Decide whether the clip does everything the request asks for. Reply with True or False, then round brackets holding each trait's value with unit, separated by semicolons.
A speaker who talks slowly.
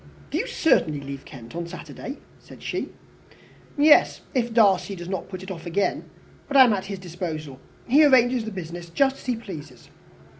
False (185 wpm)